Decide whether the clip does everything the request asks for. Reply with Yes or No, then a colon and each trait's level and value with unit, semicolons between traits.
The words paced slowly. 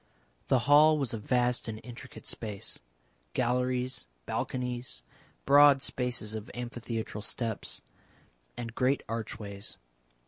Yes: slow, 105 wpm